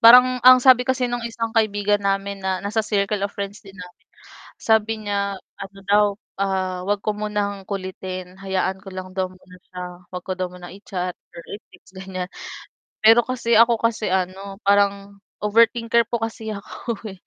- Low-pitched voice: No, high, 200 Hz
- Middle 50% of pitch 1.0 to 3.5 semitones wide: Yes, average, 2.9 semitones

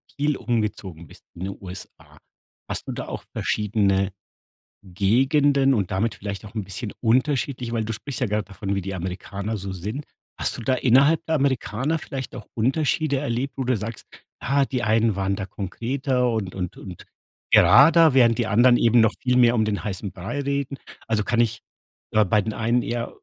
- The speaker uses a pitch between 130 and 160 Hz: No, low, 115 Hz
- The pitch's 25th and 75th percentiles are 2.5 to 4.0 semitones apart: No, average, 4.7 semitones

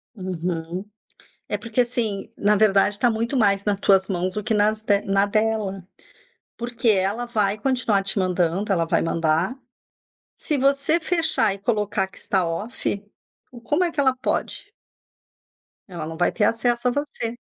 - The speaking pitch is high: Yes, high, 210 Hz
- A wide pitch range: No, average, 3.8 semitones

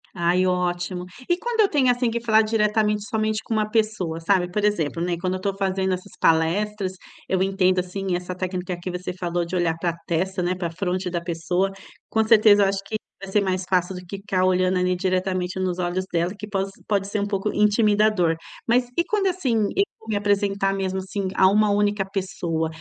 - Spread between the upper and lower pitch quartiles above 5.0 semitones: No, average, 2.7 semitones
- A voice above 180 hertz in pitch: Yes, high, 190 Hz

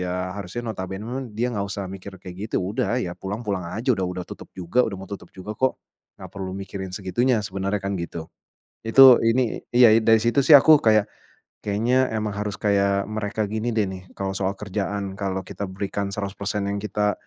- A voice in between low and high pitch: No, low, 100 Hz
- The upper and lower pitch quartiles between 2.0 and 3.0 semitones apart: Yes, narrow, 2.6 semitones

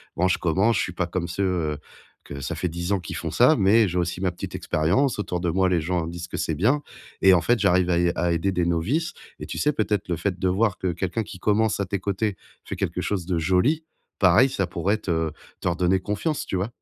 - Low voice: Yes, very low, 90 Hz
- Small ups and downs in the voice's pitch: No, average, 3.0 semitones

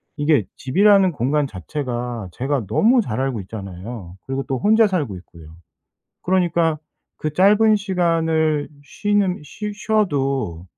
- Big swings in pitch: Yes, wide, 7.7 semitones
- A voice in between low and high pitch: Yes, medium, 150 Hz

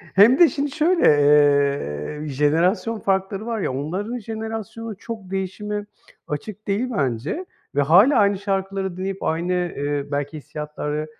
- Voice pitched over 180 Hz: Yes, high, 190 Hz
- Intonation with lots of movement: Yes, wide, 6.5 semitones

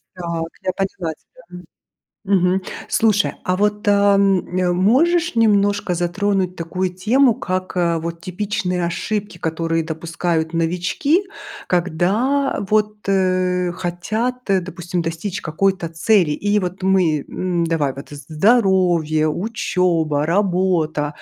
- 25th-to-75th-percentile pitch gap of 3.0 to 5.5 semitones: Yes, average, 3.3 semitones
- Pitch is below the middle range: No, medium, 180 Hz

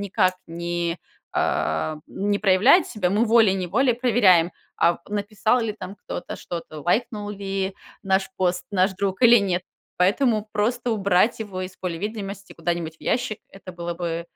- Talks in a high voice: Yes, high, 195 Hz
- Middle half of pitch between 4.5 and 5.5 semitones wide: No, average, 3.2 semitones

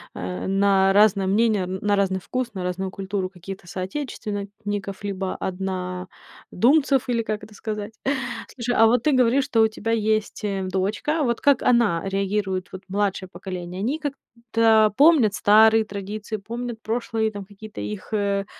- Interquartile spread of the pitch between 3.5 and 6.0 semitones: No, average, 2.9 semitones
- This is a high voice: Yes, high, 205 Hz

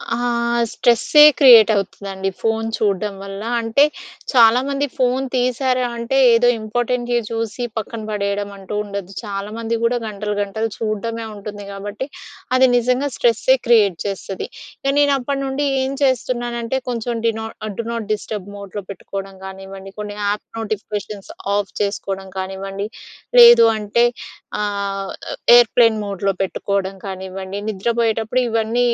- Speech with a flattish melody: No, average, 3.2 semitones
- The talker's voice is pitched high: Yes, high, 220 Hz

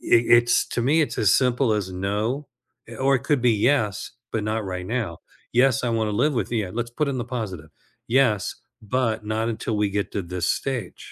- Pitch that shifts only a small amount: No, average, 3.4 semitones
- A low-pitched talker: Yes, low, 115 Hz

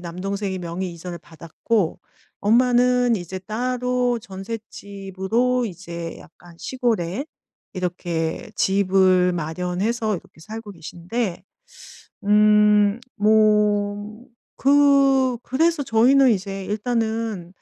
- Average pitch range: Yes, average, 4.6 semitones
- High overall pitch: Yes, high, 205 Hz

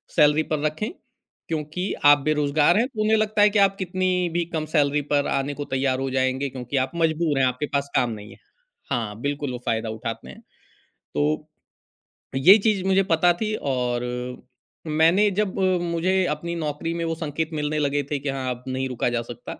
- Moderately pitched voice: Yes, medium, 150 Hz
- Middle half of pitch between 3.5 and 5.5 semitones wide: Yes, average, 4.5 semitones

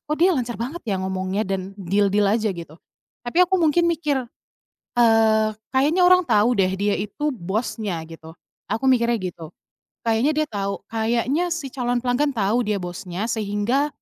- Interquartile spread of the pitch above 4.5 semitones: Yes, wide, 5.6 semitones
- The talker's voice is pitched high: Yes, high, 225 Hz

